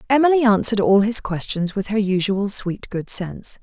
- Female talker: Yes, female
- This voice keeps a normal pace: Yes, average, 180 wpm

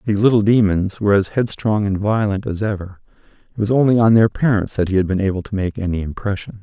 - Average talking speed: No, fast, 225 wpm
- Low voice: Yes, low, 100 Hz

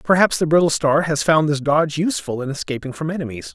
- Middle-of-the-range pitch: Yes, medium, 150 Hz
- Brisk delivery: Yes, fast, 220 wpm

